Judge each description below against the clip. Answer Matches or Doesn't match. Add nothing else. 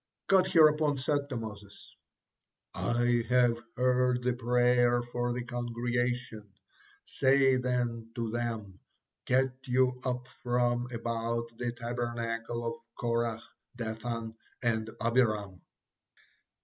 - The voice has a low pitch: Matches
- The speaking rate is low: Matches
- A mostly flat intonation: Matches